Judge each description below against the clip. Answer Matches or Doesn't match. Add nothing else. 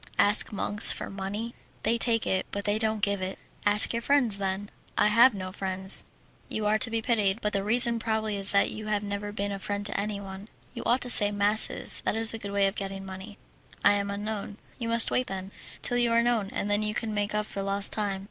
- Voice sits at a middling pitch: Doesn't match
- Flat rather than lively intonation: Matches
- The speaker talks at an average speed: Doesn't match